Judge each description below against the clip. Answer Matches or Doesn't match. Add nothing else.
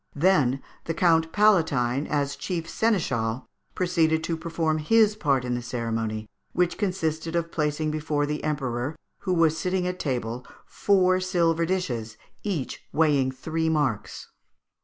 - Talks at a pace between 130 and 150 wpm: Matches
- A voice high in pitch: Doesn't match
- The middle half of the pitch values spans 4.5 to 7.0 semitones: Matches